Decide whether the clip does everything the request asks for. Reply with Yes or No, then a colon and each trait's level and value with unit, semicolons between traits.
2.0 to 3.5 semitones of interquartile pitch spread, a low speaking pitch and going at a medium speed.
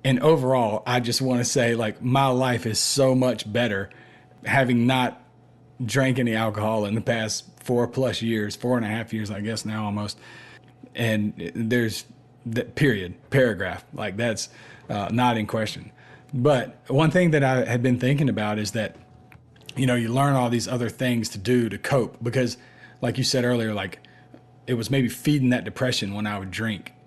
Yes: narrow, 2.6 semitones; low, 120 Hz; average, 185 wpm